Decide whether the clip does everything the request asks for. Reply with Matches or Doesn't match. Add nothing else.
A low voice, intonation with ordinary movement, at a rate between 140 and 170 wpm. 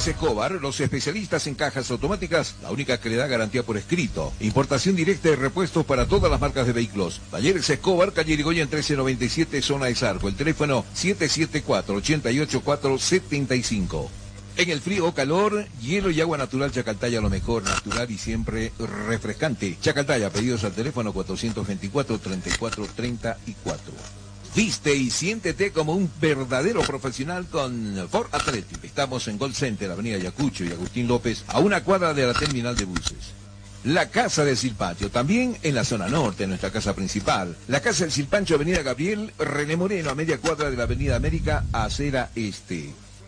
Doesn't match